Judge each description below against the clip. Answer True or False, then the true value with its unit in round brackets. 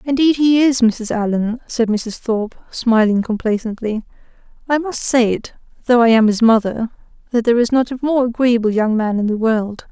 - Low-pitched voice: False (235 Hz)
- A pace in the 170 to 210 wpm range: True (190 wpm)